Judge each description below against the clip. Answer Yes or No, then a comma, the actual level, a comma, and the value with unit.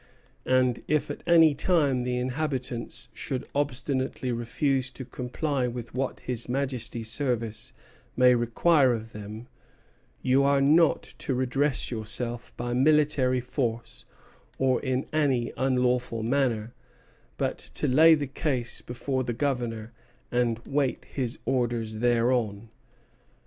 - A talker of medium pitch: No, low, 125 Hz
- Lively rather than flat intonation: No, narrow, 2.5 semitones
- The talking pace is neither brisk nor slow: No, slow, 125 wpm